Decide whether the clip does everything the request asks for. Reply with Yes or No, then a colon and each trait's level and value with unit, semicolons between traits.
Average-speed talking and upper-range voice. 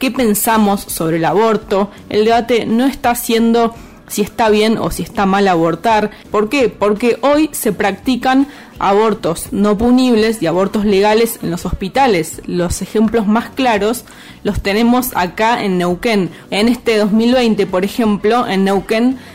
Yes: average, 150 wpm; high, 220 Hz